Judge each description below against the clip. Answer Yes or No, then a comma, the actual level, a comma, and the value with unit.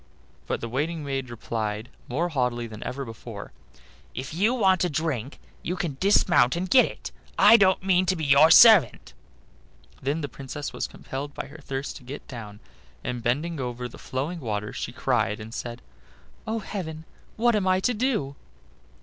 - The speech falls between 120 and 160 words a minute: No, average, 175 wpm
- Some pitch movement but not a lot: No, wide, 6.6 semitones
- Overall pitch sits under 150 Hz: Yes, medium, 140 Hz